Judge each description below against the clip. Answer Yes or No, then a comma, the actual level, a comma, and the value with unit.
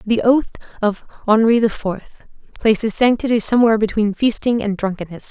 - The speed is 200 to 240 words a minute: No, average, 145 wpm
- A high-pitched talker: Yes, high, 220 Hz